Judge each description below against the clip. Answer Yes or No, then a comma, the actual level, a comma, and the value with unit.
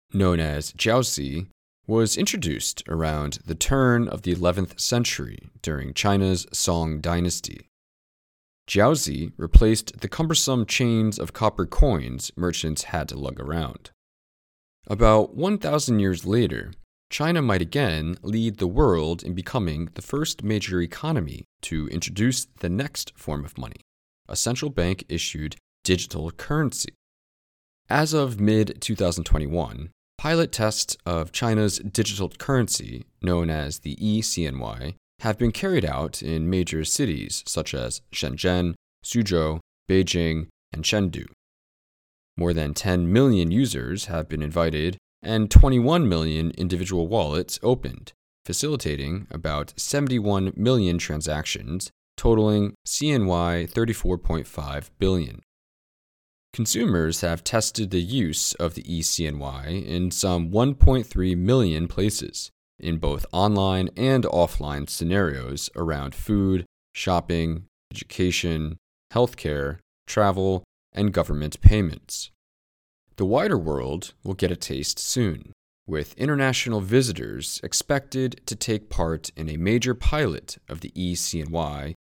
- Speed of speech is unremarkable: No, slow, 115 wpm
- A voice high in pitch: No, very low, 90 Hz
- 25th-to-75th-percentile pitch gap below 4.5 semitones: No, wide, 5.5 semitones